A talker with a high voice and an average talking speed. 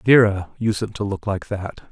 No: low, 100 Hz; average, 190 wpm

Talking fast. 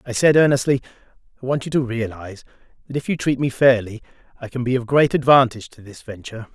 Yes: fast, 210 wpm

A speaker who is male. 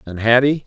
Yes: male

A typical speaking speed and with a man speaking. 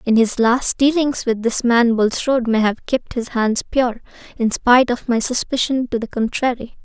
No: average, 195 wpm; female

